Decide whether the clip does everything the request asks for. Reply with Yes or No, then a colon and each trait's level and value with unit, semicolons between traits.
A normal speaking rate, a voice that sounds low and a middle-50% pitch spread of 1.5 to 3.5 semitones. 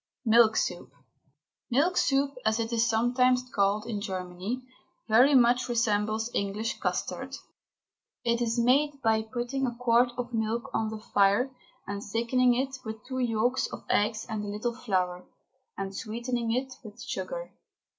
No: average, 150 wpm; high, 230 Hz; narrow, 2.6 semitones